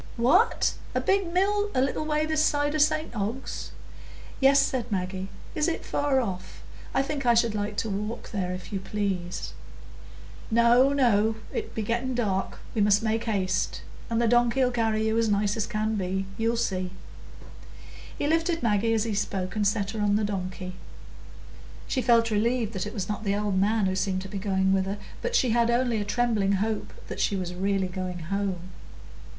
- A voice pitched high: Yes, high, 215 Hz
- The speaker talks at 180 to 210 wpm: Yes, average, 190 wpm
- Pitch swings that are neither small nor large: Yes, average, 3.7 semitones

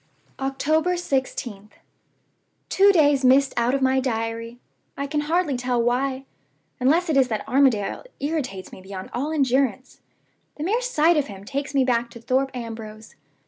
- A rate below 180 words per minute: Yes, average, 155 wpm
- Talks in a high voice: Yes, very high, 265 Hz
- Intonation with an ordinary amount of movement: Yes, average, 3.7 semitones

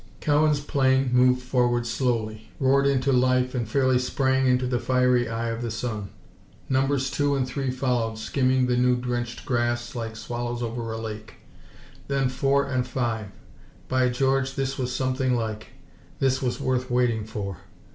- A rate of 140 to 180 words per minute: Yes, average, 160 wpm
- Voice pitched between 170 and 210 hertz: No, low, 125 Hz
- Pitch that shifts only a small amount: Yes, narrow, 1.8 semitones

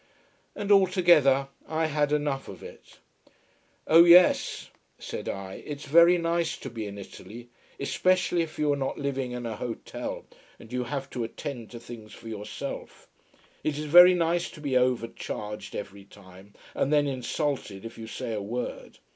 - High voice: No, low, 135 Hz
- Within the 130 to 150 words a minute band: No, average, 165 wpm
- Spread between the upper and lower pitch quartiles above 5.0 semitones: Yes, wide, 5.6 semitones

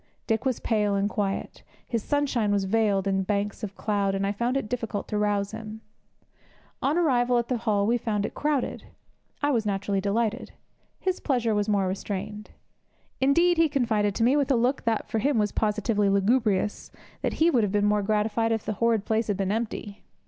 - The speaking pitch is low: No, high, 215 Hz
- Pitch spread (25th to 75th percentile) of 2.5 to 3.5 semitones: Yes, average, 2.9 semitones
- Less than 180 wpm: No, average, 200 wpm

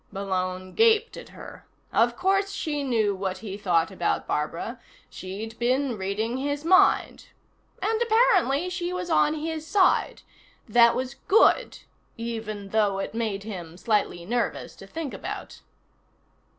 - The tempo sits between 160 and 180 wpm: No, slow, 135 wpm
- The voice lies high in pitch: Yes, high, 235 Hz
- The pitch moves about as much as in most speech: No, wide, 8.8 semitones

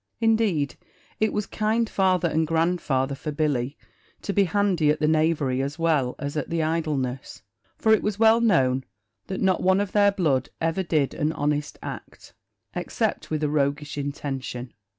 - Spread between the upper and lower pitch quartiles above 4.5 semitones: Yes, average, 5.0 semitones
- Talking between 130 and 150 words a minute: No, average, 170 wpm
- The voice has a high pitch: No, medium, 155 Hz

